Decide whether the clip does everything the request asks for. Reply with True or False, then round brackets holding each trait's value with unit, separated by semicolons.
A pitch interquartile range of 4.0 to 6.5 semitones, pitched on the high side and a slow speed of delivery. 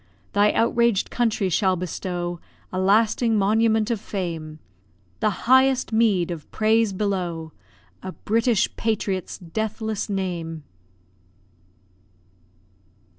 False (3.6 semitones; 205 Hz; 95 wpm)